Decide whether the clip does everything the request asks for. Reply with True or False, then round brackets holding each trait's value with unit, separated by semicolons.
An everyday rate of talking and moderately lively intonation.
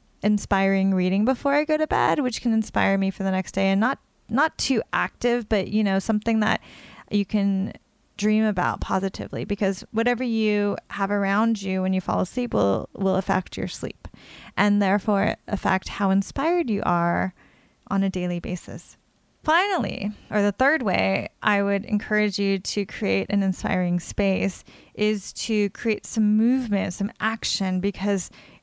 False (165 wpm; 2.1 semitones)